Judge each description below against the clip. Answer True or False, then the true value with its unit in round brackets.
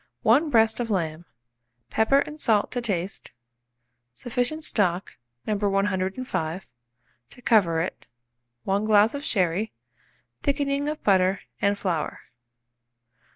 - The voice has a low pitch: False (205 Hz)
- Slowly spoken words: True (110 wpm)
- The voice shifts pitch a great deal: False (4.8 semitones)